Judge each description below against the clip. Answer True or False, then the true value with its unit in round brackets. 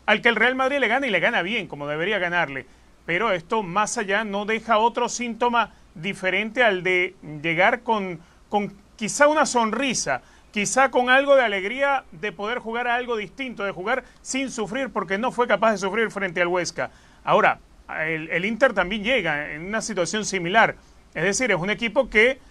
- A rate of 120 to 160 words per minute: False (190 wpm)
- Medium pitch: False (215 Hz)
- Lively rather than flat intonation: False (4.5 semitones)